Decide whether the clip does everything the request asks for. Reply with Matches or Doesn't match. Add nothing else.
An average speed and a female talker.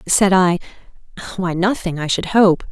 Matches